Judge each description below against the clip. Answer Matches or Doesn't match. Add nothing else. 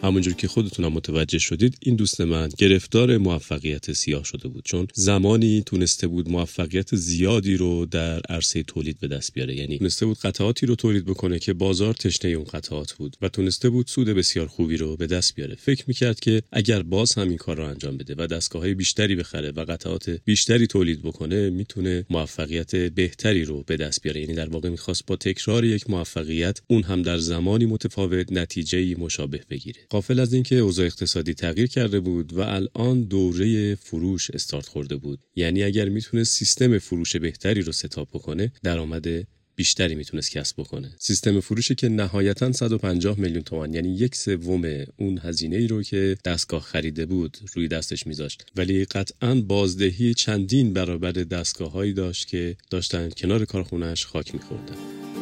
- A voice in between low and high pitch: Doesn't match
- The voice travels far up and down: Doesn't match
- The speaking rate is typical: Doesn't match